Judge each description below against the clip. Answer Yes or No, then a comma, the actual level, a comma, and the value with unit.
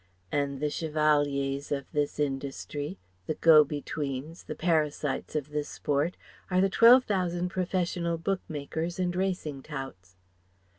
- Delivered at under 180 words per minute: Yes, slow, 135 wpm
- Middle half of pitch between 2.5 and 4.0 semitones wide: Yes, average, 3.6 semitones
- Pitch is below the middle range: No, medium, 150 Hz